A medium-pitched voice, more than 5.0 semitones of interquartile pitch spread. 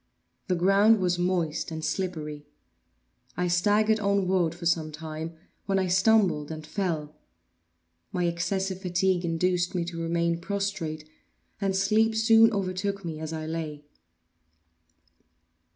No: medium, 180 Hz; average, 3.3 semitones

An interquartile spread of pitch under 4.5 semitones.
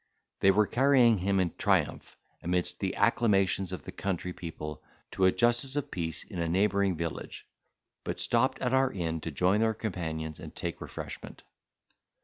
No: average, 4.8 semitones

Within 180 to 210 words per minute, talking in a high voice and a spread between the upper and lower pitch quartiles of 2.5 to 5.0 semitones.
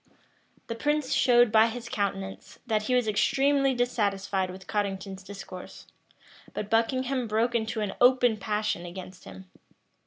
No: slow, 135 wpm; high, 220 Hz; average, 3.9 semitones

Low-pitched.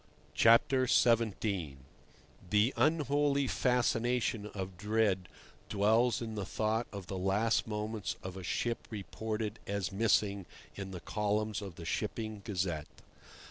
Yes: low, 105 Hz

